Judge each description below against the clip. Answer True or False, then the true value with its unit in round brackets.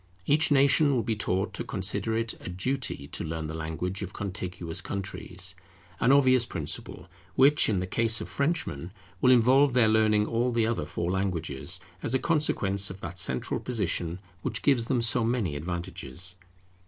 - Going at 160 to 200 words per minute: True (170 wpm)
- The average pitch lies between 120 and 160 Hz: False (100 Hz)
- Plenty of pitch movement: True (5.7 semitones)